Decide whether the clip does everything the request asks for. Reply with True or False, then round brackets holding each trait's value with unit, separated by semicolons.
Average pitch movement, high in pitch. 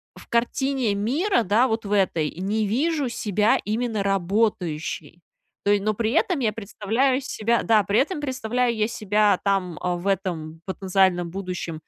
True (3.9 semitones; 210 Hz)